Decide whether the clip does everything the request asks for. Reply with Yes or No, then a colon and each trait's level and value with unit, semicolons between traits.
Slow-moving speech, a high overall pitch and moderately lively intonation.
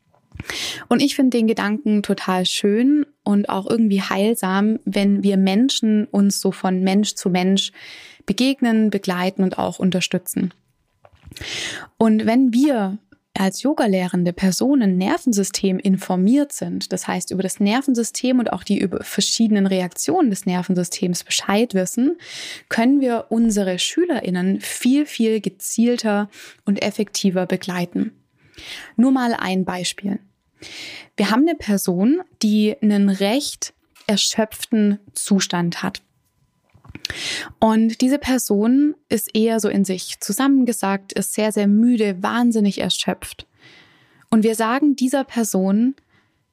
Yes: slow, 120 wpm; high, 210 Hz; average, 3.7 semitones